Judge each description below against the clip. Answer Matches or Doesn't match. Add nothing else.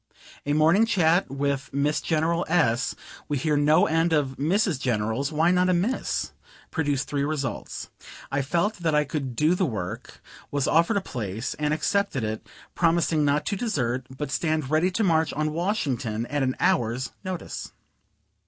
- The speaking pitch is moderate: Matches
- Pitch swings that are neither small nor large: Matches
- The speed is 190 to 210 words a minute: Doesn't match